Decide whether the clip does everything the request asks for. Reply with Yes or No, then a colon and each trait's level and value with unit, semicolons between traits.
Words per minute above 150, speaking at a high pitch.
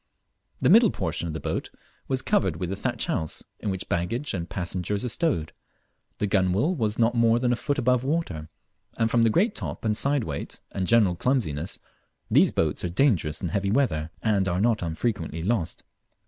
No: average, 190 wpm; low, 105 Hz